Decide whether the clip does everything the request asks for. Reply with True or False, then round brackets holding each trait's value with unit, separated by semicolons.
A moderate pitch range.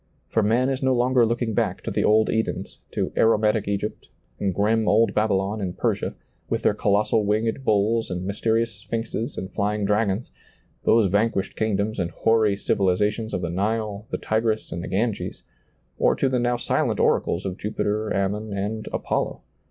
False (2.0 semitones)